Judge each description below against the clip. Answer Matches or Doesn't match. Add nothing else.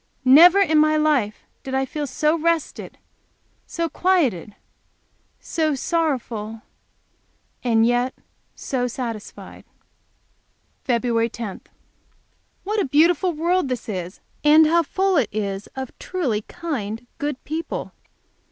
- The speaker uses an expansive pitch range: Matches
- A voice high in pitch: Matches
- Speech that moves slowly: Matches